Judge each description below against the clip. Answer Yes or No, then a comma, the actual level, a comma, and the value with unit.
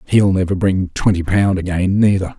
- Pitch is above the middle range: No, very low, 95 Hz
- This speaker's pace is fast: No, average, 175 wpm